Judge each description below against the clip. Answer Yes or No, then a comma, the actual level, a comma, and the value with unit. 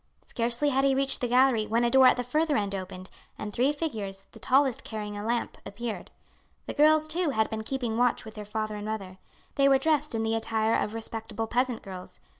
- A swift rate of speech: Yes, fast, 220 wpm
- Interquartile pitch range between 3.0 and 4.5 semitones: Yes, average, 3.8 semitones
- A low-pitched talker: No, high, 230 Hz